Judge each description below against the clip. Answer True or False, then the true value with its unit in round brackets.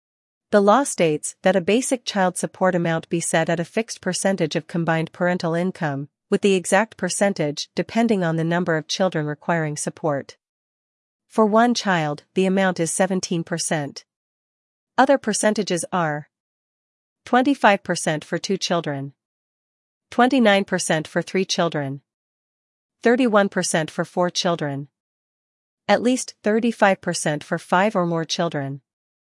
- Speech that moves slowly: True (125 wpm)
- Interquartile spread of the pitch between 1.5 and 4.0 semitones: True (3.5 semitones)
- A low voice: False (180 Hz)